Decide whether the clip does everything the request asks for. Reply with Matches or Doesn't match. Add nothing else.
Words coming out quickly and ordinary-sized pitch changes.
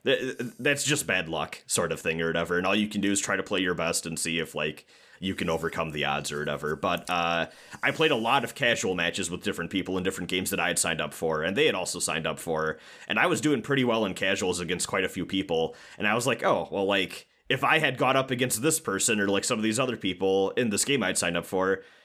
Doesn't match